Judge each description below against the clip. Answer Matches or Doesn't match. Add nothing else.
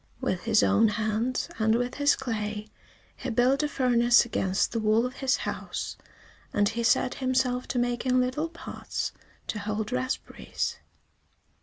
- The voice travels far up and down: Doesn't match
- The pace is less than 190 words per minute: Matches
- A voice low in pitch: Doesn't match